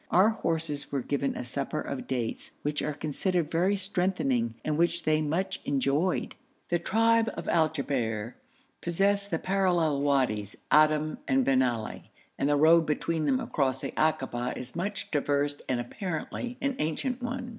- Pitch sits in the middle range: Yes, medium, 155 Hz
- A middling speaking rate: Yes, average, 160 wpm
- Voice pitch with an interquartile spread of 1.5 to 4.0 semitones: No, average, 4.9 semitones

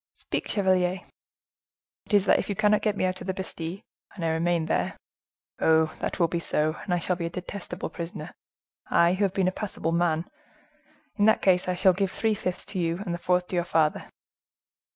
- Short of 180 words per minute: No, average, 200 wpm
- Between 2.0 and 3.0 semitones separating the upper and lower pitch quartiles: Yes, average, 2.7 semitones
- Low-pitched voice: No, medium, 180 Hz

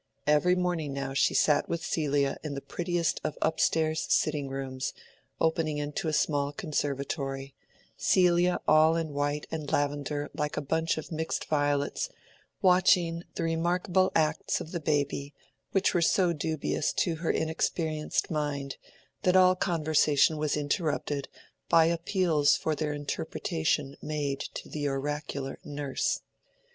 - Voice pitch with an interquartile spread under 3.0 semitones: Yes, narrow, 2.4 semitones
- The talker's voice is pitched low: No, medium, 155 Hz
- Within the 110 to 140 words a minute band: Yes, slow, 135 wpm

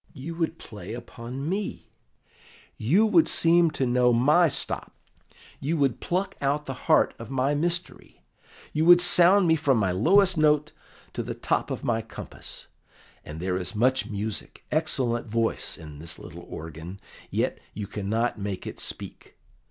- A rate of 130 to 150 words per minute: No, average, 160 wpm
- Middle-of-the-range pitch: No, low, 130 Hz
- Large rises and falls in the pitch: Yes, wide, 7.0 semitones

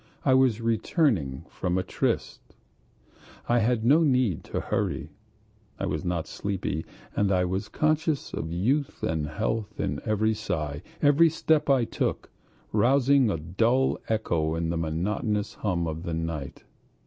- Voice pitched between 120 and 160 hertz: No, low, 105 Hz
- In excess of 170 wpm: No, average, 150 wpm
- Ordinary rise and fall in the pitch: No, wide, 7.4 semitones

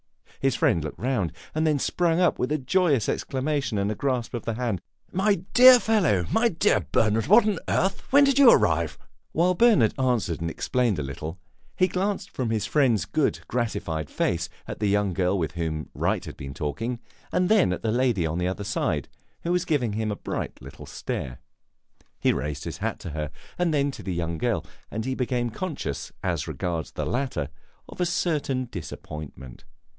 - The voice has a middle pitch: No, low, 120 Hz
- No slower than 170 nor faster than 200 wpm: Yes, average, 190 wpm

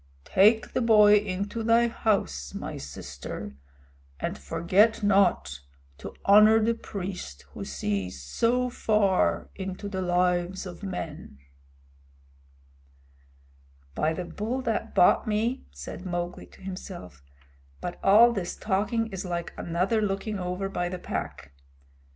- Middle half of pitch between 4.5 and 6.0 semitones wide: No, average, 3.6 semitones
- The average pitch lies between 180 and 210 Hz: Yes, high, 190 Hz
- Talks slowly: Yes, slow, 125 wpm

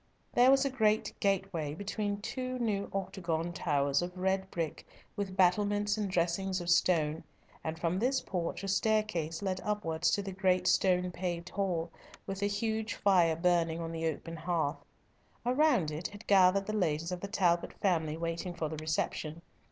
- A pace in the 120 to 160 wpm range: No, average, 170 wpm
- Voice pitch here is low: No, medium, 185 Hz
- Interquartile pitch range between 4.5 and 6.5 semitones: No, average, 3.5 semitones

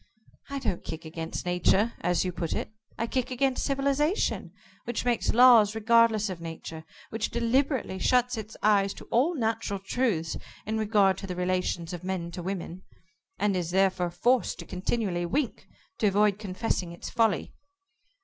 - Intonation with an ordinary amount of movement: Yes, average, 4.7 semitones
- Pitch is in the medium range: No, high, 205 Hz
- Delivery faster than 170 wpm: No, average, 160 wpm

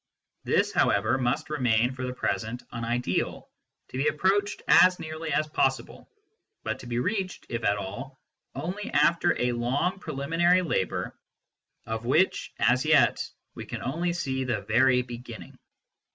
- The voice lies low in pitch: Yes, low, 130 Hz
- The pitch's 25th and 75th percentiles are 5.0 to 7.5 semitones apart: Yes, wide, 5.5 semitones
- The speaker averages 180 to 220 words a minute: No, average, 155 wpm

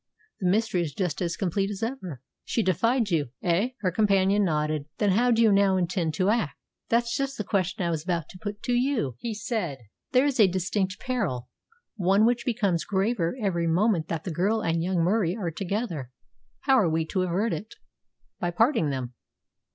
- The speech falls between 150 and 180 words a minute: No, average, 195 wpm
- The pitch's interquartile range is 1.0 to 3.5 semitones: No, average, 4.8 semitones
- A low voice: No, high, 190 Hz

